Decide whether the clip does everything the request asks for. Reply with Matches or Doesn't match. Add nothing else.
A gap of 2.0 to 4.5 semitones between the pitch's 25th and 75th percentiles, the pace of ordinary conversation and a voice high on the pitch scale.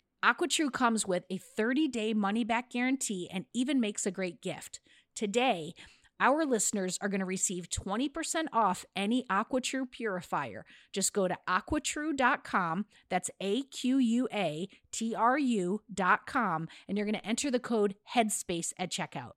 Doesn't match